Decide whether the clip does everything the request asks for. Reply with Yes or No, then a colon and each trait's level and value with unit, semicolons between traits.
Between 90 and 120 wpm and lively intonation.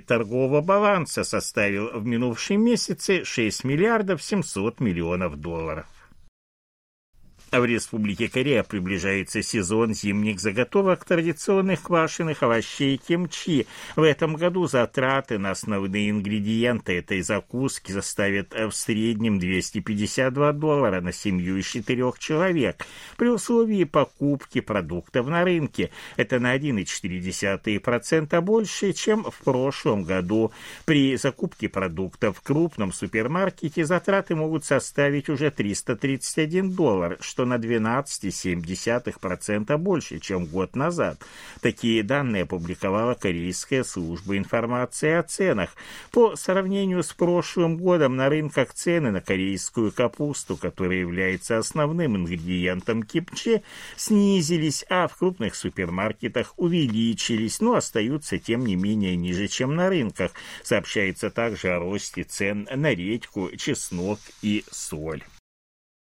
Yes: slow, 110 wpm; wide, 8.1 semitones